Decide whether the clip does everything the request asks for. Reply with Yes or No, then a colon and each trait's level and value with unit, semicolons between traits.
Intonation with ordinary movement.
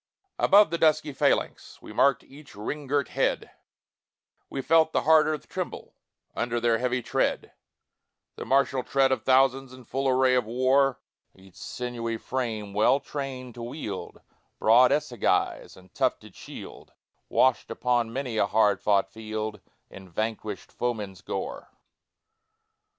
Yes: average, 3.7 semitones